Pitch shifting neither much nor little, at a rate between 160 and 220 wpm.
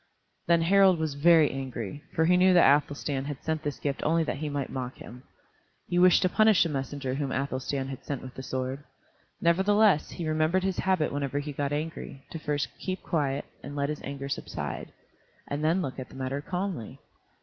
Yes: average, 3.7 semitones; average, 200 wpm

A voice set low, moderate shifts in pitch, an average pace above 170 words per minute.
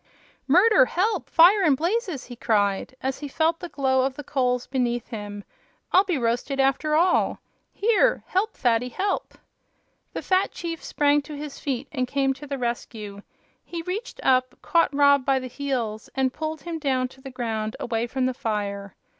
No: very high, 270 Hz; average, 5.0 semitones; average, 180 wpm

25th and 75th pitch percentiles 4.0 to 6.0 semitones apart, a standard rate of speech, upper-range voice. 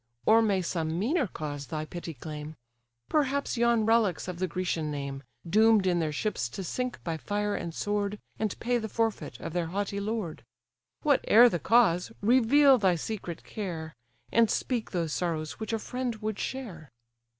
Yes: wide, 5.6 semitones; average, 170 wpm; high, 200 Hz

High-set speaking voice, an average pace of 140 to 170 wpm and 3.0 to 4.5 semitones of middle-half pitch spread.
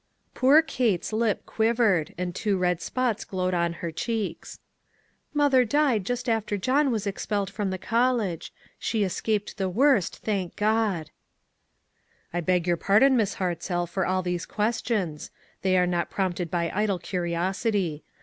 Yes: high, 195 Hz; average, 160 wpm; average, 4.2 semitones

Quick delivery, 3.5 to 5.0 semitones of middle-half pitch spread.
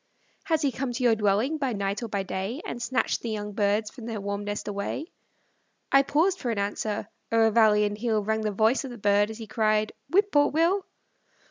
Yes: fast, 220 wpm; average, 4.1 semitones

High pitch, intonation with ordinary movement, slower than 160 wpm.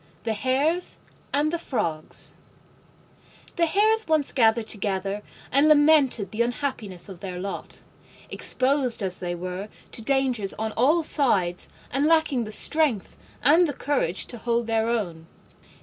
No: high, 235 Hz; wide, 6.6 semitones; average, 140 wpm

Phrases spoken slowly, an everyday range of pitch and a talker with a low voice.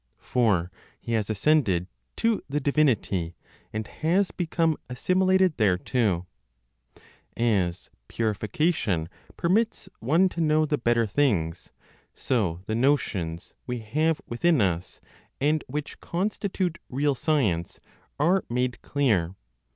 No: slow, 110 wpm; wide, 7.5 semitones; low, 125 Hz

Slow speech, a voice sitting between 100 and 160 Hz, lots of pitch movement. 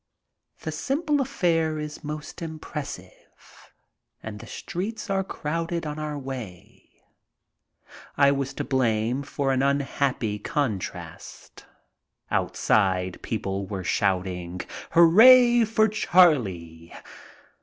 Yes: slow, 110 wpm; medium, 140 Hz; wide, 8.3 semitones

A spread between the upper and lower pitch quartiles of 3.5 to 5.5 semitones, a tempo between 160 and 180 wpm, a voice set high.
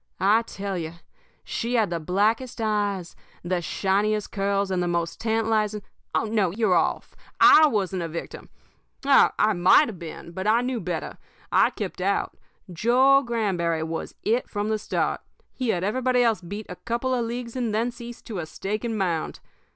Yes: average, 4.3 semitones; average, 175 wpm; high, 210 Hz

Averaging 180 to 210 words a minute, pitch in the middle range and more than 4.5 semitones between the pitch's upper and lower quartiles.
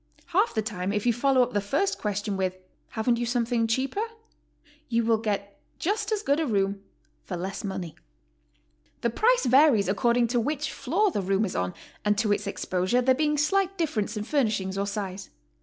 No: average, 190 wpm; high, 230 Hz; wide, 5.6 semitones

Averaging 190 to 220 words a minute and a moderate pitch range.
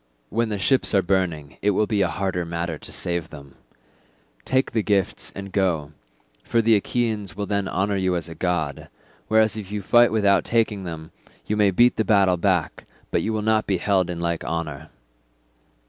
Yes: average, 195 wpm; average, 3.9 semitones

